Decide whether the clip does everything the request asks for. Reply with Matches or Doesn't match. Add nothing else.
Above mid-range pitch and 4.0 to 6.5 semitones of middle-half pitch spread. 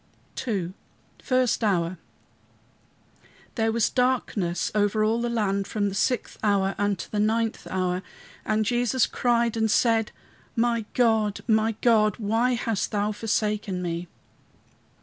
Doesn't match